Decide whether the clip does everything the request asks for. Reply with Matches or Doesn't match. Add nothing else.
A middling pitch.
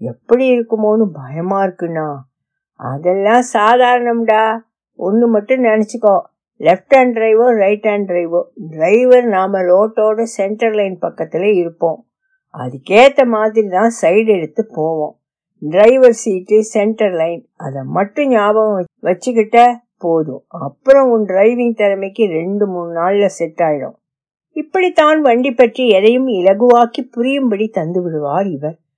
Doesn't match